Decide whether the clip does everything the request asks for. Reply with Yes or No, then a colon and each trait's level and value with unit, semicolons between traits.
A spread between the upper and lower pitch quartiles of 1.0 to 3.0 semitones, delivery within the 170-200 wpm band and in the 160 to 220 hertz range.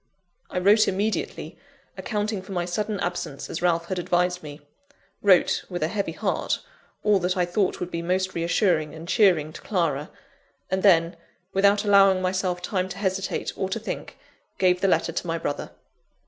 Yes: narrow, 2.4 semitones; average, 175 wpm; medium, 185 Hz